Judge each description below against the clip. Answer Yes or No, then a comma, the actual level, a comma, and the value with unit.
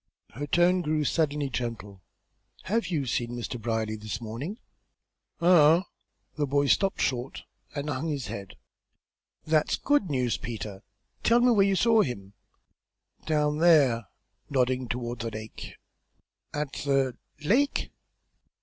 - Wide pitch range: Yes, wide, 5.7 semitones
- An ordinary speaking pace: No, slow, 130 wpm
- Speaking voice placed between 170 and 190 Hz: No, medium, 140 Hz